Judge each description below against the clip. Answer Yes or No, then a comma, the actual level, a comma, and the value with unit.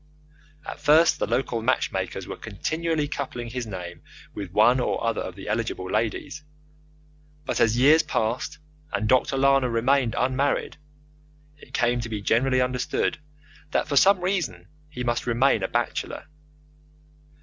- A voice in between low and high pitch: No, low, 125 Hz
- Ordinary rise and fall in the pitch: Yes, average, 3.5 semitones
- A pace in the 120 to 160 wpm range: Yes, average, 145 wpm